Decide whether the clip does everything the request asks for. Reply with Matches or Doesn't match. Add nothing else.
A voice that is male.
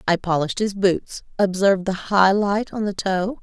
Doesn't match